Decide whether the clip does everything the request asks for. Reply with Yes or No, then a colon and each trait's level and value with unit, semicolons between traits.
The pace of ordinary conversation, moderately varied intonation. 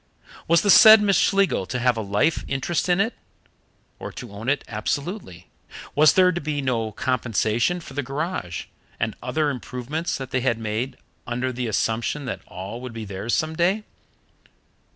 No: average, 170 wpm; wide, 6.1 semitones